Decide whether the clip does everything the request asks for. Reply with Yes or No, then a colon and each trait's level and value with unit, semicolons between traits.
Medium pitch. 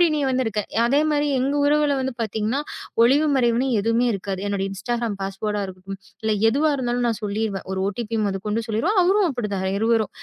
No: high, 230 Hz